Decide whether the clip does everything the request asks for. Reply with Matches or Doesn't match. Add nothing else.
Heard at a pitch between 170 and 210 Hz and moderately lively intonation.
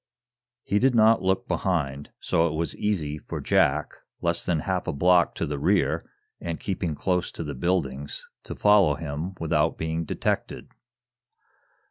Doesn't match